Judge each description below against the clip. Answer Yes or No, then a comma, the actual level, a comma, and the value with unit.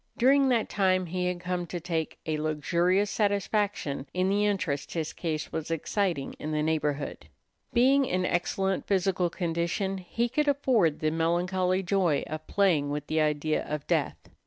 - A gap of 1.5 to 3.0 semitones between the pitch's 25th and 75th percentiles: No, average, 4.1 semitones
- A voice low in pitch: No, medium, 180 Hz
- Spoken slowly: No, average, 160 wpm